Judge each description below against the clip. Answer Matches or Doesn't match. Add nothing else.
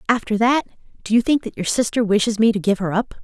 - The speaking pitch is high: Matches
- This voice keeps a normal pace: Doesn't match